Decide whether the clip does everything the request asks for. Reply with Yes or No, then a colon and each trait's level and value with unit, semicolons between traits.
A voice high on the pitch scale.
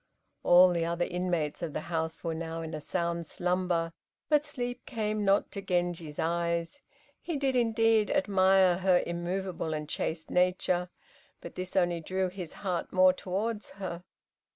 No: medium, 180 Hz